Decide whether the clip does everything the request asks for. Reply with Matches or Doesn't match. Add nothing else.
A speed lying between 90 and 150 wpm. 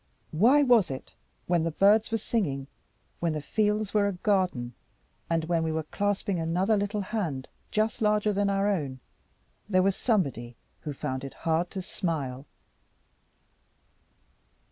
Matches